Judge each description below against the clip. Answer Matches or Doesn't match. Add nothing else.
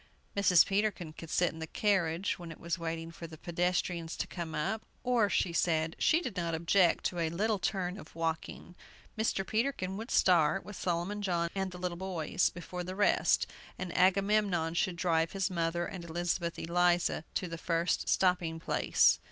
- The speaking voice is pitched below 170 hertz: Doesn't match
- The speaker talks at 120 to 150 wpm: Doesn't match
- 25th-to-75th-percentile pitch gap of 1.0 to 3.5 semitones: Matches